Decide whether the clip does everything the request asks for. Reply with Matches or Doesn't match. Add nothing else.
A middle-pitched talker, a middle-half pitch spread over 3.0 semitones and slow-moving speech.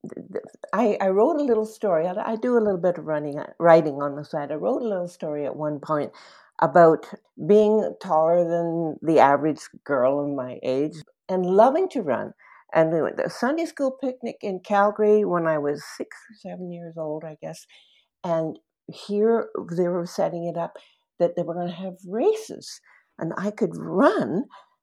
Doesn't match